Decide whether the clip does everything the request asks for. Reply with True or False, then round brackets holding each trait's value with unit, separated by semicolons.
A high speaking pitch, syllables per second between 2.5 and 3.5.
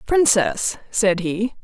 True (220 Hz; 3.1 syllables/s)